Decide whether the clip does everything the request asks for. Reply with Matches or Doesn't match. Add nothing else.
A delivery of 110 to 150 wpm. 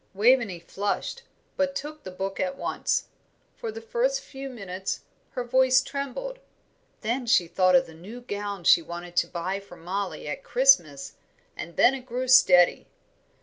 Doesn't match